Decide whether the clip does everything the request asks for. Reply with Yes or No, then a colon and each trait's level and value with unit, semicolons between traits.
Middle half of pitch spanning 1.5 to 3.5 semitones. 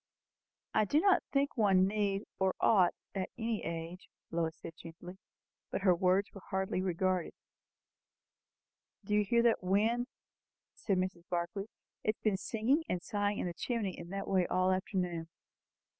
Yes: average, 2.7 semitones